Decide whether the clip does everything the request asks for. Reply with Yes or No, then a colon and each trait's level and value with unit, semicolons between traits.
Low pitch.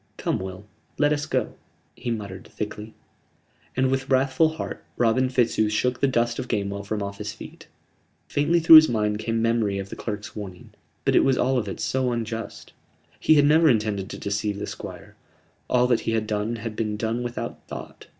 Yes: low, 115 Hz